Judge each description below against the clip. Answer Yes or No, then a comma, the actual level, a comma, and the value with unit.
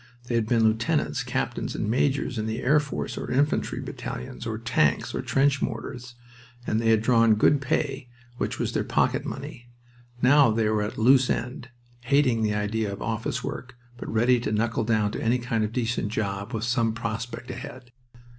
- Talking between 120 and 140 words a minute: No, average, 190 wpm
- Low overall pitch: Yes, low, 115 Hz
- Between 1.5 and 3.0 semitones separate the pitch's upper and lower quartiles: Yes, narrow, 2.4 semitones